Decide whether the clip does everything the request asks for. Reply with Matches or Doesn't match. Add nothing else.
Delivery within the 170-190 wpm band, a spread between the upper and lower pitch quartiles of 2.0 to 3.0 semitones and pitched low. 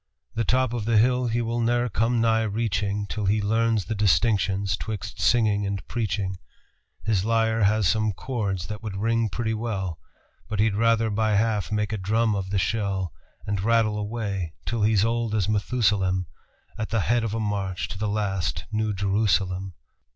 Matches